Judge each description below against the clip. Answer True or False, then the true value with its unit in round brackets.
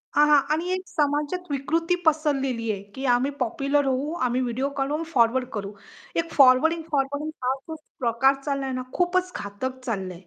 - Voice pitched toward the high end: True (275 Hz)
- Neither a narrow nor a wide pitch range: True (3.3 semitones)